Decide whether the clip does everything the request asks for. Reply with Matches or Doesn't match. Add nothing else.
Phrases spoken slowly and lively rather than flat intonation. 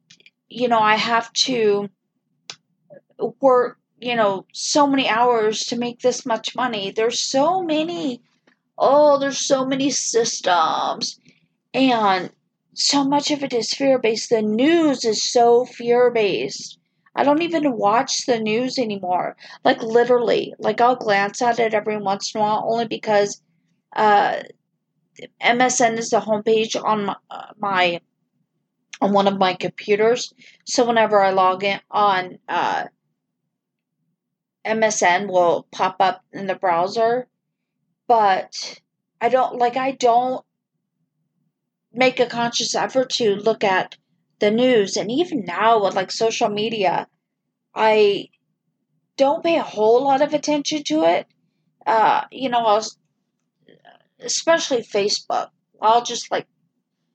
Doesn't match